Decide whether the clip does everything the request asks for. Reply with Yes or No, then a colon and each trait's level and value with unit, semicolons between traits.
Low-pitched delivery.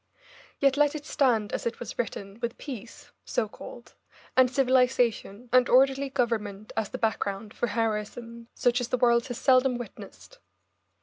No: high, 240 Hz